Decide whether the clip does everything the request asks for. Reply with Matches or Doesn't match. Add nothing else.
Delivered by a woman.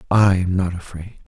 Doesn't match